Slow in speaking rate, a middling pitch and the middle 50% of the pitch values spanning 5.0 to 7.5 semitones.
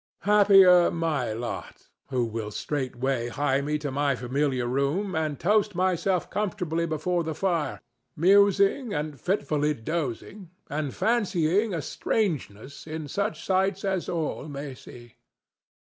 Yes: slow, 130 wpm; medium, 155 Hz; wide, 5.5 semitones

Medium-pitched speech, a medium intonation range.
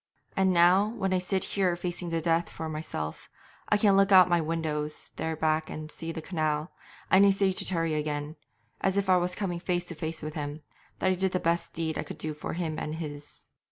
Yes: medium, 165 Hz; average, 3.1 semitones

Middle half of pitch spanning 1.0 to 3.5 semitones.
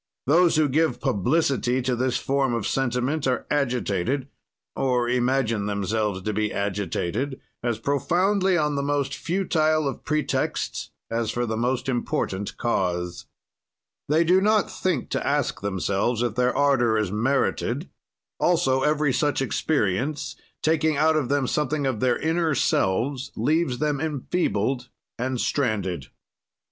No: average, 4.7 semitones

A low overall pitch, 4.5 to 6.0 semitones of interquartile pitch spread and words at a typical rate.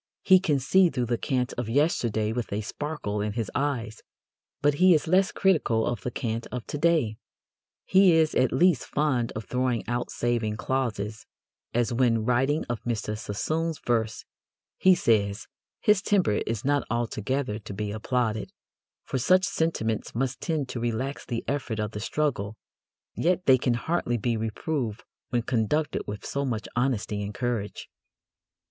Yes: low, 120 Hz; average, 4.8 semitones; average, 165 wpm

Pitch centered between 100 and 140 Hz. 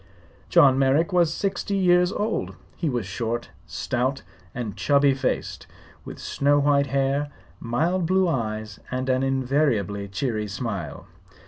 Yes: low, 135 Hz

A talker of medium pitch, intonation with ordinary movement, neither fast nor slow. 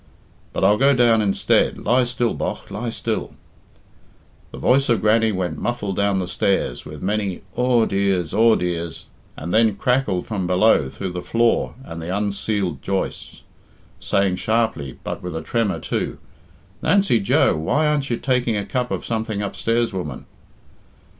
No: low, 105 Hz; average, 4.3 semitones; average, 160 wpm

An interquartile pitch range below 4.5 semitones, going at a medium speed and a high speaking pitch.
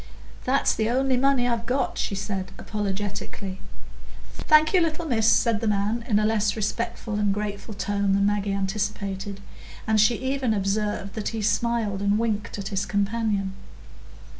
Yes: narrow, 2.6 semitones; average, 160 wpm; high, 210 Hz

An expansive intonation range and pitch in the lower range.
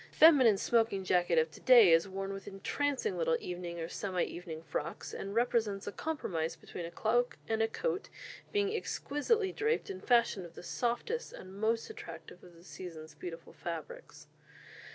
No: wide, 7.4 semitones; high, 200 Hz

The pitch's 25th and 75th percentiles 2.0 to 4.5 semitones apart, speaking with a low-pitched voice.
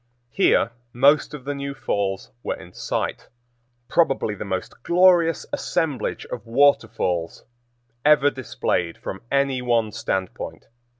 No: wide, 5.6 semitones; low, 125 Hz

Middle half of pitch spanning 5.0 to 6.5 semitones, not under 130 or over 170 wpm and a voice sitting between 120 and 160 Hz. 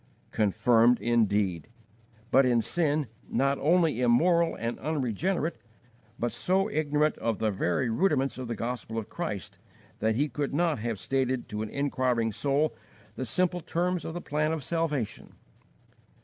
Yes: wide, 5.4 semitones; average, 150 wpm; low, 135 Hz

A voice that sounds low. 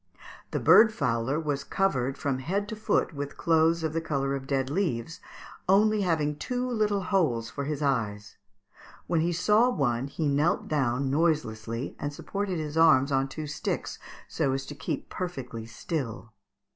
No: medium, 150 Hz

